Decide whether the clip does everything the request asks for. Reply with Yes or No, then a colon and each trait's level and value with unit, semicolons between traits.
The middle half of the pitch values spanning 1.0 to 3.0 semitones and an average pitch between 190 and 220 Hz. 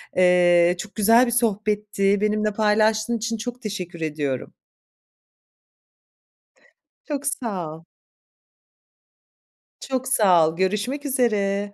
No: average, 4.0 semitones; high, 210 Hz